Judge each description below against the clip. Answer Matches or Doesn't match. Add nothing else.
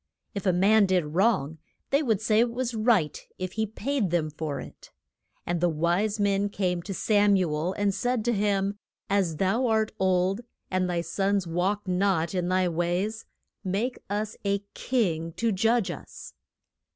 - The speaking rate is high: Doesn't match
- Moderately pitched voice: Doesn't match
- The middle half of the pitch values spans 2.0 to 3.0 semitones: Doesn't match